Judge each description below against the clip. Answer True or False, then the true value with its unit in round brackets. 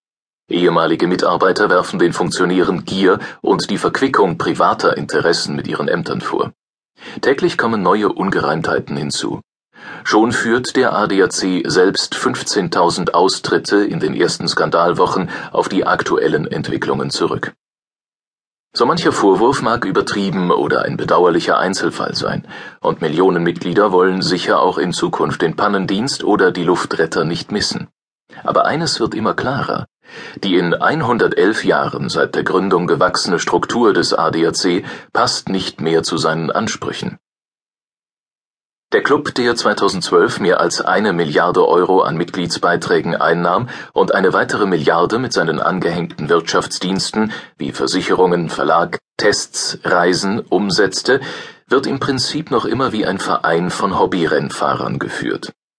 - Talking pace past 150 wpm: False (130 wpm)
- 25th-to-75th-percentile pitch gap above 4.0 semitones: False (3.7 semitones)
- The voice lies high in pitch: False (90 Hz)